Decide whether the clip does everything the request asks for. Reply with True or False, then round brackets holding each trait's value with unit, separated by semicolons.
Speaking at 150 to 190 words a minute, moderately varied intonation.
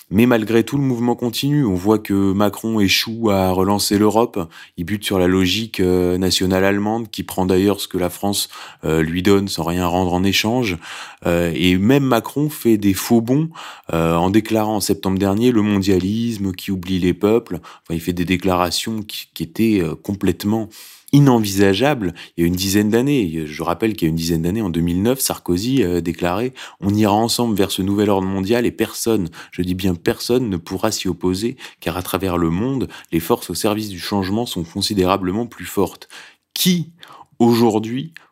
True (180 wpm; 3.7 semitones)